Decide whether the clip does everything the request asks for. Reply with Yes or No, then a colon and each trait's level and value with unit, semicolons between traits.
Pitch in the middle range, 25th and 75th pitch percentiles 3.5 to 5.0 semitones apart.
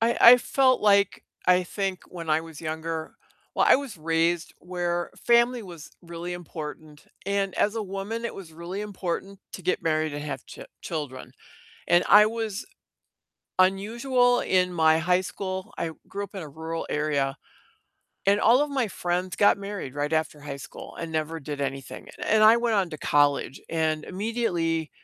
Yes: medium, 180 Hz; average, 4.3 semitones